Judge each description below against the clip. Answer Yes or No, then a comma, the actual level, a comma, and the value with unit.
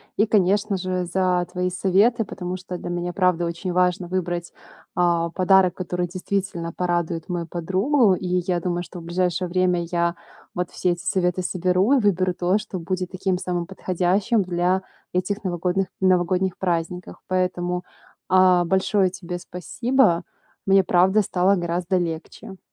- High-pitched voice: No, medium, 180 Hz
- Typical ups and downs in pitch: No, narrow, 1.3 semitones